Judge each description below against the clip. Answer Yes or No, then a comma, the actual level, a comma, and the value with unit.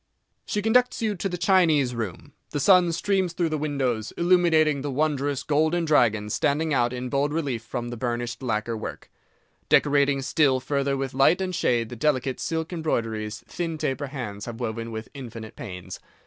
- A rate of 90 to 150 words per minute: No, average, 175 wpm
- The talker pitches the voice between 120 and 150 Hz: Yes, medium, 140 Hz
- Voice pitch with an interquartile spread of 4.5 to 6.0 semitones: Yes, average, 5.2 semitones